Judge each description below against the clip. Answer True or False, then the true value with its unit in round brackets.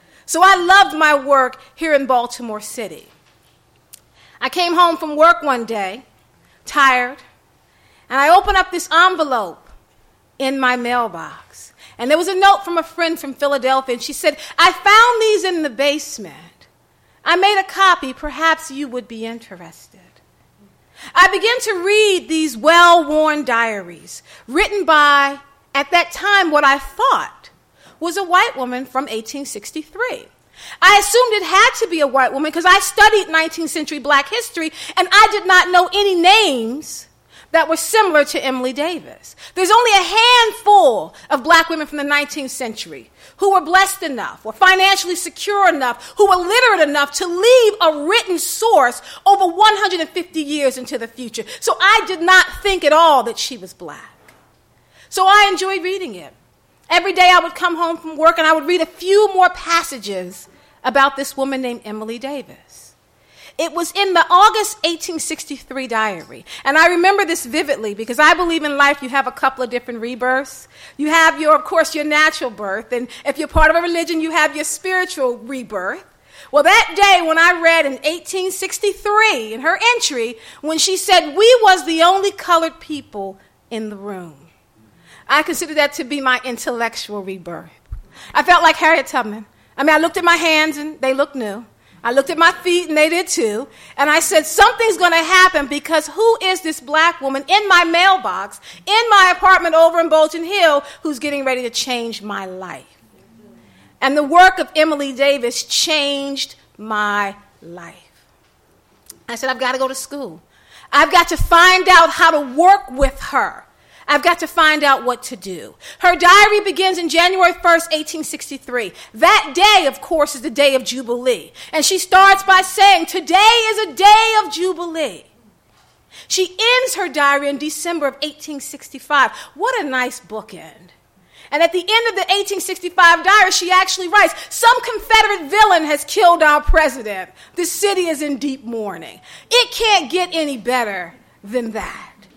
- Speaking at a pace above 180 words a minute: False (175 wpm)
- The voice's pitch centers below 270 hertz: False (320 Hz)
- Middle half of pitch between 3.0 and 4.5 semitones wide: False (5.4 semitones)